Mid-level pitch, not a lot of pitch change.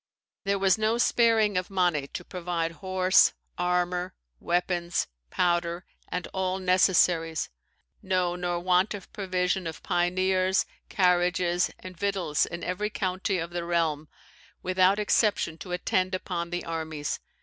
Yes: medium, 180 Hz; narrow, 1.5 semitones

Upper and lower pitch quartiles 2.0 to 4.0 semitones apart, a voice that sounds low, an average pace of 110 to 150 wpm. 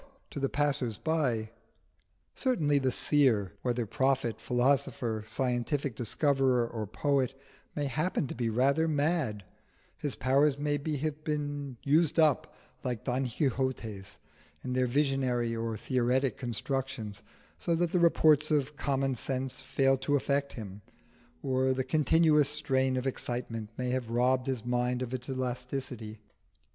Yes: average, 2.9 semitones; low, 130 Hz; slow, 135 wpm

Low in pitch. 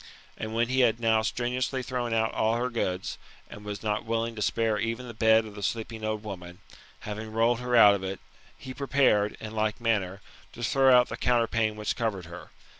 Yes: low, 110 Hz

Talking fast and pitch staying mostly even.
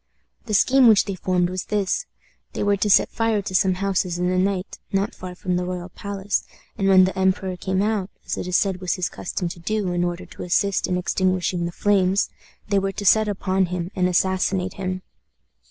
Yes: fast, 215 wpm; narrow, 1.7 semitones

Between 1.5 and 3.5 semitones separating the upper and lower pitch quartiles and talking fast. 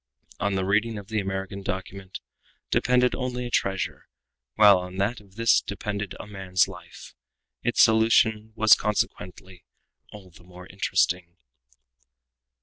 No: average, 2.7 semitones; average, 140 wpm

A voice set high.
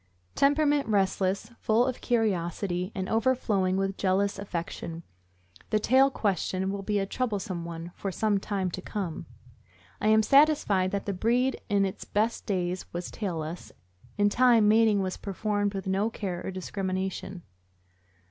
Yes: high, 200 Hz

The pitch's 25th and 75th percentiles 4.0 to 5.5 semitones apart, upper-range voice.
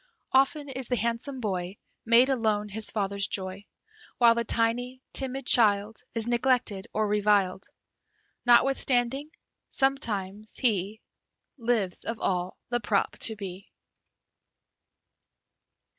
No: average, 3.6 semitones; high, 225 Hz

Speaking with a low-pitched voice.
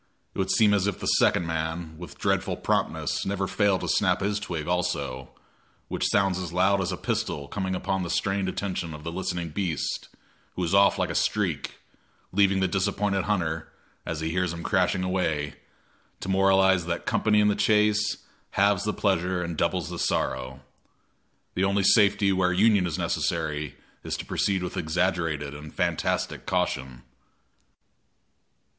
Yes: very low, 90 Hz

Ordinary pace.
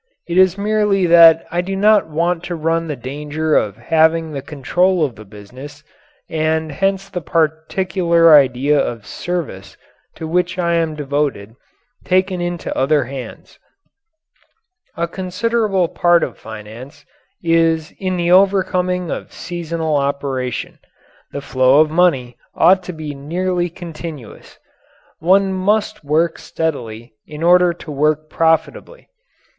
No: slow, 130 wpm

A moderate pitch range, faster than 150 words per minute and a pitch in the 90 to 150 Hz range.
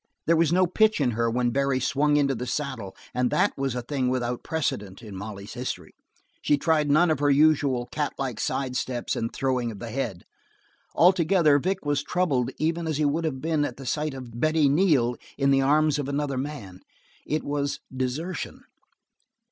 Yes: average, 3.7 semitones; average, 190 wpm; medium, 140 Hz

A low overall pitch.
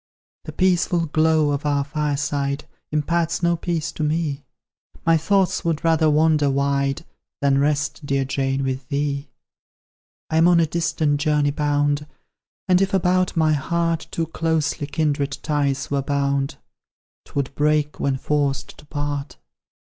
No: medium, 150 Hz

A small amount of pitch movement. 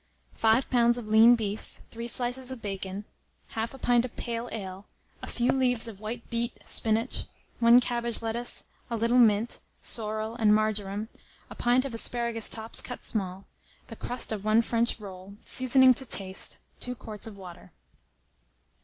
Yes: narrow, 2.2 semitones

